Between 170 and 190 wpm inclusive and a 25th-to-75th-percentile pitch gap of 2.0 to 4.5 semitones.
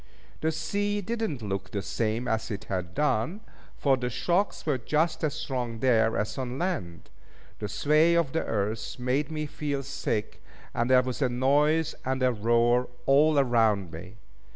No: average, 175 wpm; average, 5.2 semitones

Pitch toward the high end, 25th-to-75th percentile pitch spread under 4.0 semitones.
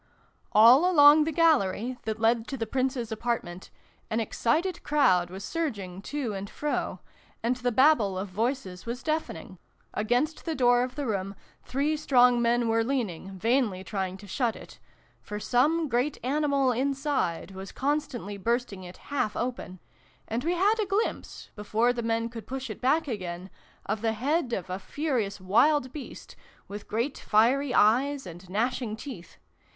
No: high, 240 Hz; average, 5.2 semitones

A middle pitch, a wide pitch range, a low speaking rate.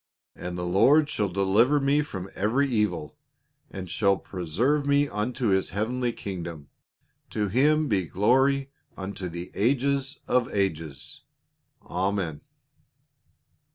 No: low, 105 Hz; wide, 6.5 semitones; slow, 120 wpm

